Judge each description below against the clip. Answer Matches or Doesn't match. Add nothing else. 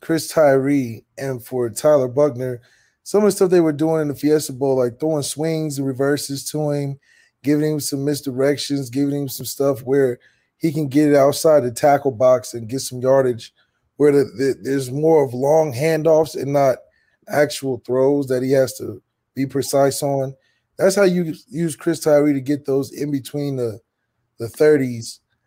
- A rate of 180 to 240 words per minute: Matches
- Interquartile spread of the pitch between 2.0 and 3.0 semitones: Matches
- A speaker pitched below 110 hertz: Doesn't match